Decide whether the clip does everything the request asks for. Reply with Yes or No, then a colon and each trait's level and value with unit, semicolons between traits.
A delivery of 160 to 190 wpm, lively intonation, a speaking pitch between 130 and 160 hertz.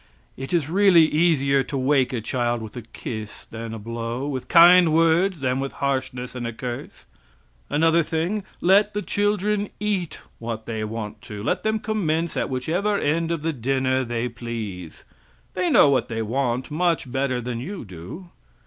Yes: average, 175 wpm; wide, 6.2 semitones; low, 135 Hz